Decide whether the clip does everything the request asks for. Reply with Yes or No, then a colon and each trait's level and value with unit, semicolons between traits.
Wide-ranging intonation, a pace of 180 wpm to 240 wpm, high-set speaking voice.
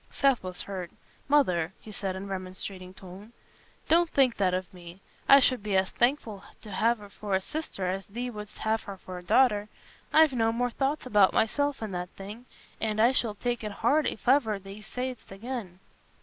No: average, 4.6 semitones; fast, 205 wpm; high, 210 Hz